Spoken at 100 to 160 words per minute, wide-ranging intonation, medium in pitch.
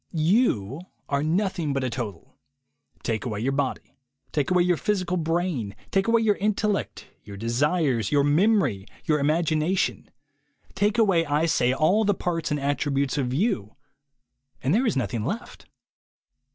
Yes: average, 150 wpm; wide, 6.6 semitones; medium, 155 Hz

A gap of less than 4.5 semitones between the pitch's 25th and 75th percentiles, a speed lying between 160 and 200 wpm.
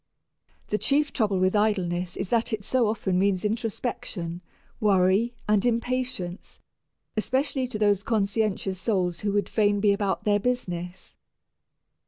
No: average, 3.7 semitones; slow, 135 wpm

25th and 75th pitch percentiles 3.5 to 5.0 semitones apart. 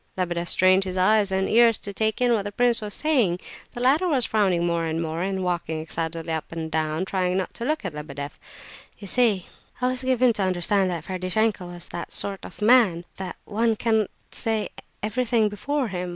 Yes: average, 4.6 semitones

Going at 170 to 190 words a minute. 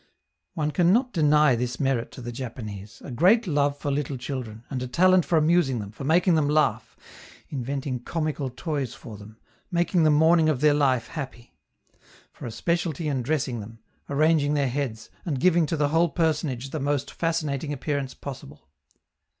Yes: average, 175 wpm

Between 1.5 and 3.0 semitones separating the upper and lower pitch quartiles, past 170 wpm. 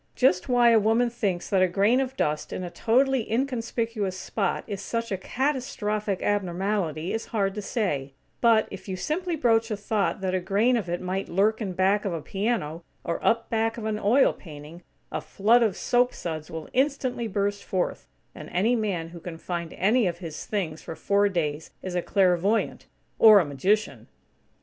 No: average, 4.3 semitones; average, 190 wpm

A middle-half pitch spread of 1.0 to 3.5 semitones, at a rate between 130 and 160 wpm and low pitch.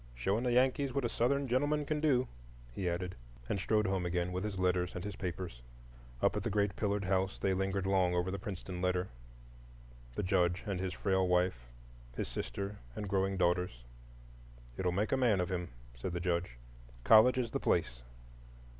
No: average, 2.8 semitones; average, 180 wpm; very low, 95 Hz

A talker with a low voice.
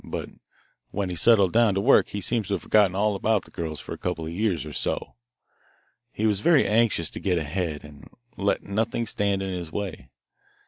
Yes: low, 100 Hz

